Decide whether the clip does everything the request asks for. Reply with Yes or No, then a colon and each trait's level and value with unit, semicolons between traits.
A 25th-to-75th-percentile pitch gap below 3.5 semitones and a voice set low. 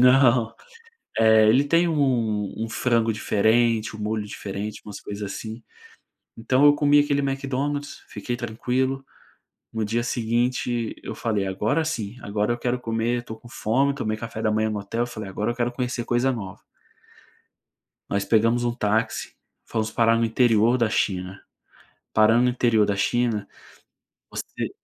Yes: narrow, 2.5 semitones; low, 115 Hz